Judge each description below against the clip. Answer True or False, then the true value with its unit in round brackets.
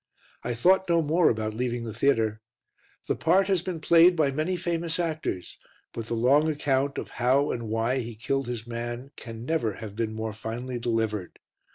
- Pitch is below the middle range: True (125 Hz)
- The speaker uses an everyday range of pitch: False (5.7 semitones)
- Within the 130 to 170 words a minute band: False (185 wpm)